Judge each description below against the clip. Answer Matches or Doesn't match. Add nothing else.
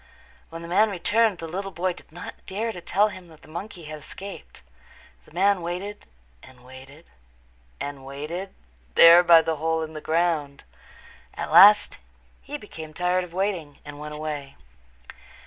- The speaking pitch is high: Doesn't match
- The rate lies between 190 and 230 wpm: Doesn't match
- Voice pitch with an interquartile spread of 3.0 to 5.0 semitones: Matches